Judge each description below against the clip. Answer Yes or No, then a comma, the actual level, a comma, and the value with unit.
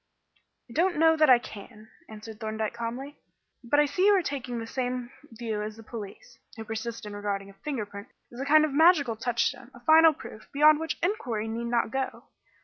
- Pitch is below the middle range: No, high, 240 Hz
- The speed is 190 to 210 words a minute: Yes, fast, 205 wpm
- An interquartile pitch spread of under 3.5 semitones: No, average, 5.1 semitones